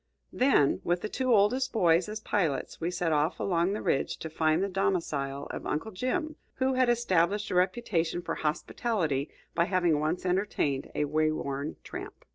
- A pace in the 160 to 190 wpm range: Yes, average, 175 wpm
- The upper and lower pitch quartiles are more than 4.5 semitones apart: Yes, average, 5.2 semitones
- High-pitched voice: No, medium, 175 Hz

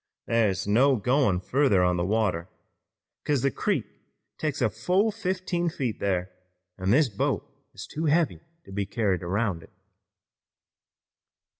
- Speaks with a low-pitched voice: Yes, low, 115 Hz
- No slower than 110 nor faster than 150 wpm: Yes, average, 145 wpm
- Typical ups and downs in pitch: No, wide, 7.4 semitones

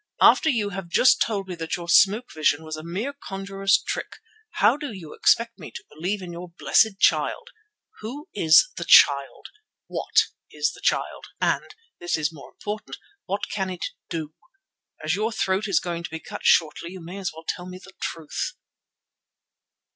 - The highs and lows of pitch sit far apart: No, average, 4.1 semitones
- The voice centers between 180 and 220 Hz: Yes, medium, 185 Hz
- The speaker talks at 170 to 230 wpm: Yes, average, 175 wpm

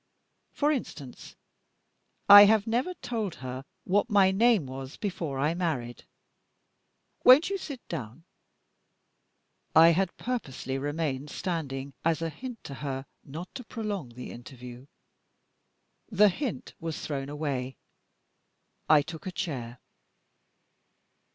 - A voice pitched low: No, medium, 165 Hz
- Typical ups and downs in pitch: No, wide, 7.4 semitones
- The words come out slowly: Yes, slow, 120 wpm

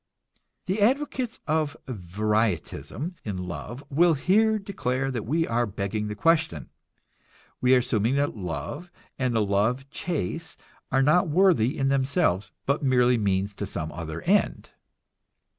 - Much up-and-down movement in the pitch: Yes, wide, 7.7 semitones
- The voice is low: Yes, low, 130 Hz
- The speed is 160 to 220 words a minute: No, average, 140 wpm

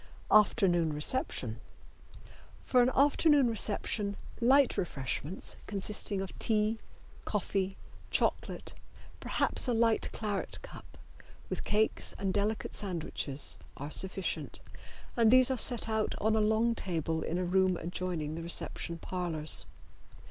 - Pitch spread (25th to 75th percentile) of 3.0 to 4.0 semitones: No, average, 4.4 semitones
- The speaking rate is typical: No, slow, 120 wpm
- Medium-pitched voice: No, high, 200 Hz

